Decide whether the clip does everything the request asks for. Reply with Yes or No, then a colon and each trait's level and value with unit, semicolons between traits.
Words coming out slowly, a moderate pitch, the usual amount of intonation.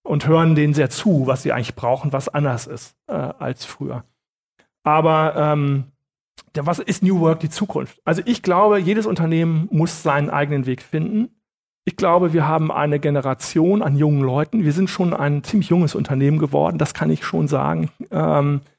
No: average, 180 wpm; medium, 155 Hz; average, 3.3 semitones